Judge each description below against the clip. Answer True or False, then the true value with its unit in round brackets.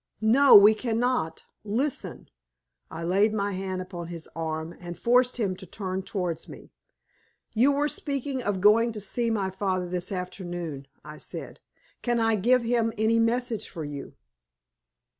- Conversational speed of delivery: True (155 wpm)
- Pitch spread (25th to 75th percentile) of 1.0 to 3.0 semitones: False (4.6 semitones)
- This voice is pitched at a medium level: False (200 Hz)